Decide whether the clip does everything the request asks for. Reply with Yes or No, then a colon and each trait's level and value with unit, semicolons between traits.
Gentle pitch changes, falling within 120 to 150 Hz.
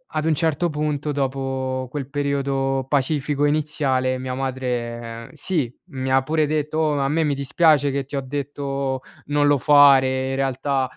Yes: narrow, 2.0 semitones; medium, 140 Hz